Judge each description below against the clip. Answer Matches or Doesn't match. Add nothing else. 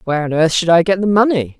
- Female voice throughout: Matches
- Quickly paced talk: Matches